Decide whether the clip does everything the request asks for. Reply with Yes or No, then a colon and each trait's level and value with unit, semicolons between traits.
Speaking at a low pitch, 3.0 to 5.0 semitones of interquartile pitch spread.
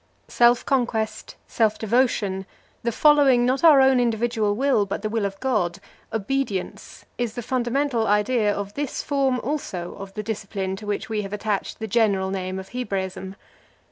No: high, 220 Hz; average, 4.1 semitones